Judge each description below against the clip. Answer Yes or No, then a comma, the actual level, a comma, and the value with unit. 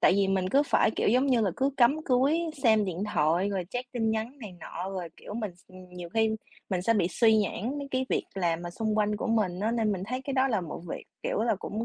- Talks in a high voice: Yes, high, 215 Hz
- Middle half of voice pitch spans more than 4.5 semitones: Yes, average, 4.9 semitones